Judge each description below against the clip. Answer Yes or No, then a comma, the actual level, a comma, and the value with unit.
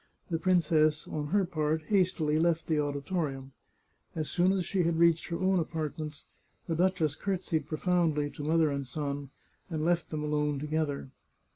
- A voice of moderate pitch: Yes, medium, 155 Hz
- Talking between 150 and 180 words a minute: Yes, average, 160 wpm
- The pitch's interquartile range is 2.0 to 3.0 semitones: Yes, narrow, 2.5 semitones